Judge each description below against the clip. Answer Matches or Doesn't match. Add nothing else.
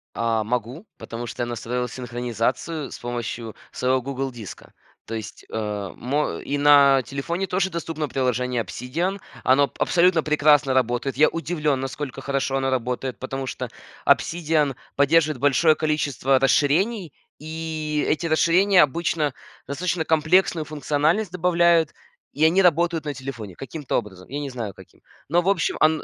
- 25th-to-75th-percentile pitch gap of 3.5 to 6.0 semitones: Matches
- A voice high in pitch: Doesn't match